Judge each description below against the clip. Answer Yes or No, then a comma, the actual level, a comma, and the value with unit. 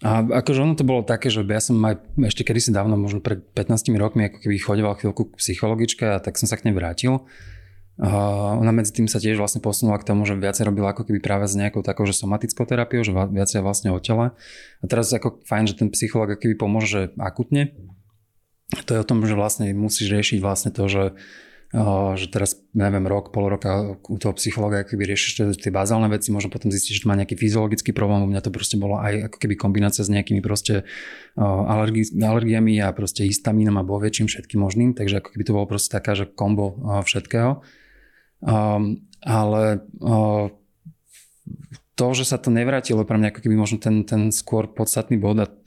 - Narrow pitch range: Yes, narrow, 2.0 semitones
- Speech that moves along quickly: Yes, fast, 205 wpm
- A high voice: No, low, 105 Hz